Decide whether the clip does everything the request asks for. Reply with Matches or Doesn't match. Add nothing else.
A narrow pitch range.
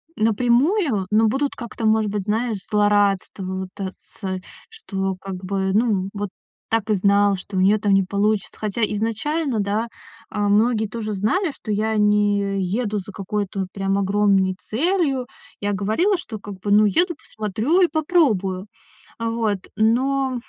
Doesn't match